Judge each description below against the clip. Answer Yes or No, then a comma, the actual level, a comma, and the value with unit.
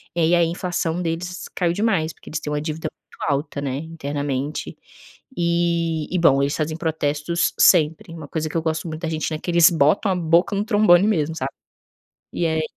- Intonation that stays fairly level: Yes, narrow, 2.3 semitones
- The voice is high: No, medium, 165 Hz